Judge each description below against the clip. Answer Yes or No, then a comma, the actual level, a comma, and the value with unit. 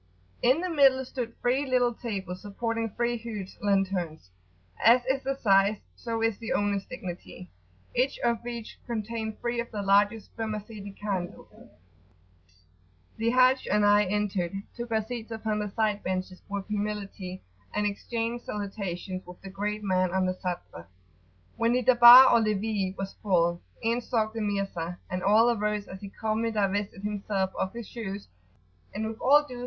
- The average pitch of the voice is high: Yes, high, 210 Hz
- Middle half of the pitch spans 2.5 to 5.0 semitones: Yes, average, 3.1 semitones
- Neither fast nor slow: Yes, average, 165 wpm